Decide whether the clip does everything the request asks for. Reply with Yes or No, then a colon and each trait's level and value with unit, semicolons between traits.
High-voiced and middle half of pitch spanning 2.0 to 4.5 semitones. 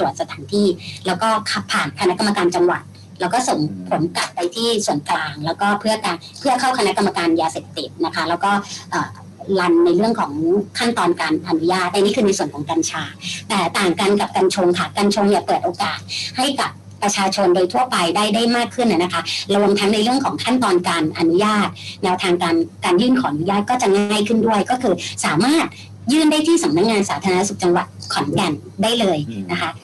Yes: high, 200 Hz; average, 4.2 semitones